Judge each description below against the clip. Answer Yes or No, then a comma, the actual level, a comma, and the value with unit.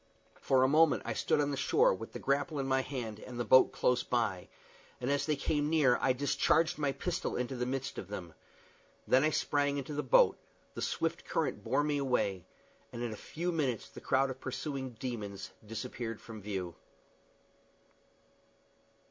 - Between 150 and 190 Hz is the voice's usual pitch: No, low, 130 Hz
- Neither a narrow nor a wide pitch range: Yes, average, 3.5 semitones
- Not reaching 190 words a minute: Yes, average, 180 wpm